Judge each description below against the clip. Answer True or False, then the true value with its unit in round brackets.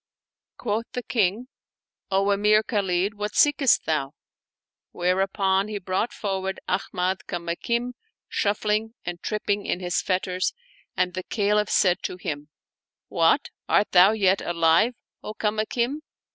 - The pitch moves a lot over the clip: False (2.8 semitones)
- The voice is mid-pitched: False (195 Hz)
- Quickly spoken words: False (140 wpm)